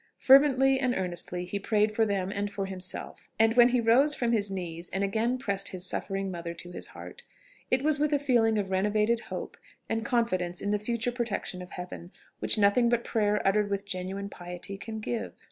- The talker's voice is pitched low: No, high, 210 Hz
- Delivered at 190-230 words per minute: Yes, average, 200 wpm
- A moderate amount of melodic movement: Yes, average, 3.7 semitones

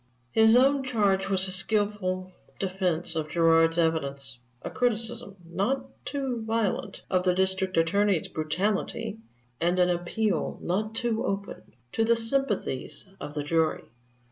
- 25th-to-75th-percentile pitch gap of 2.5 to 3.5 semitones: No, average, 4.8 semitones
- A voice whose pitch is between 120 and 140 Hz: No, high, 190 Hz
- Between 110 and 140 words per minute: Yes, slow, 135 wpm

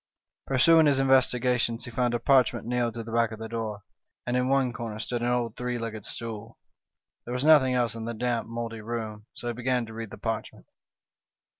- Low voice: Yes, low, 120 Hz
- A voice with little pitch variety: Yes, narrow, 1.6 semitones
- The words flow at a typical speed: No, fast, 210 wpm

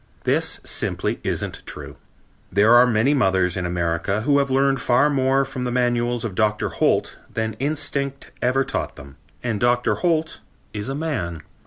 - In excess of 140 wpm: Yes, average, 165 wpm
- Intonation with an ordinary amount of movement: Yes, average, 4.6 semitones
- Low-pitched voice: Yes, low, 120 Hz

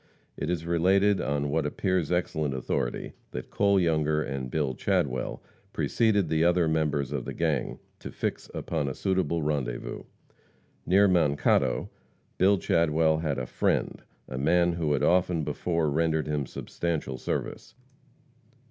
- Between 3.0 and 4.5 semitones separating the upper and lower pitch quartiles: Yes, average, 3.4 semitones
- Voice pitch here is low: Yes, very low, 80 Hz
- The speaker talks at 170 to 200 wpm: No, average, 140 wpm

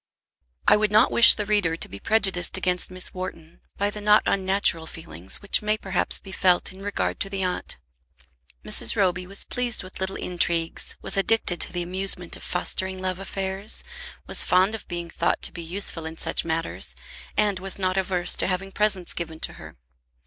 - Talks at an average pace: Yes, average, 190 wpm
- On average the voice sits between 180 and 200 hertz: Yes, medium, 185 Hz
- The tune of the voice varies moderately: No, narrow, 2.2 semitones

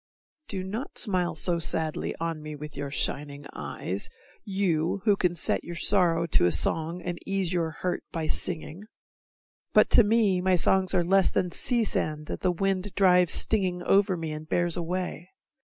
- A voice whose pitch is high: No, medium, 175 Hz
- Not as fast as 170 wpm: No, average, 175 wpm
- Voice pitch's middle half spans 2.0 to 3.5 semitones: Yes, average, 3.1 semitones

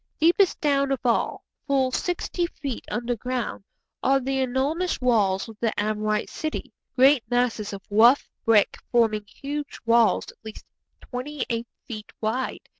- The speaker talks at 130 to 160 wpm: Yes, average, 140 wpm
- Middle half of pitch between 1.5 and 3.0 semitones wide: No, average, 3.8 semitones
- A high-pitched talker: Yes, very high, 250 Hz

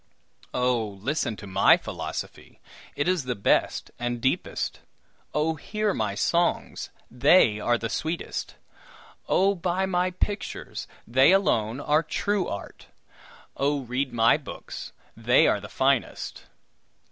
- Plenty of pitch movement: Yes, wide, 7.4 semitones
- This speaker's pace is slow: Yes, slow, 125 wpm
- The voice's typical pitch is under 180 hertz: Yes, medium, 140 Hz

